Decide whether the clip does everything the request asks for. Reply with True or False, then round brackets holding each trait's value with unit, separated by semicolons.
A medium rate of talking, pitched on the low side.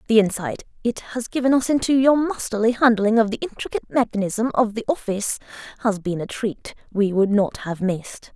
False (185 wpm; 220 Hz)